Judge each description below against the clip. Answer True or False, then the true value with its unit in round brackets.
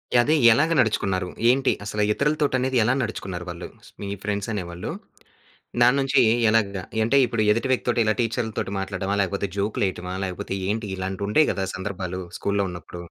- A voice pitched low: True (105 Hz)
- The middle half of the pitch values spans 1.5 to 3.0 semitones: False (4.0 semitones)